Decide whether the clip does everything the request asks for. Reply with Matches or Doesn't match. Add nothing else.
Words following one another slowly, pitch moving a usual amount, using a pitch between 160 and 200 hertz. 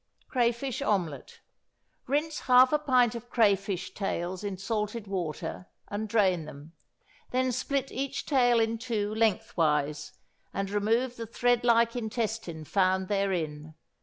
Doesn't match